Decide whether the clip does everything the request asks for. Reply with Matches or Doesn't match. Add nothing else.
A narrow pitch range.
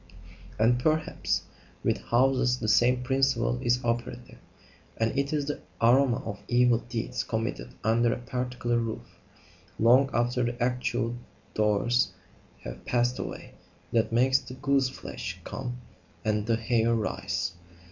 Matches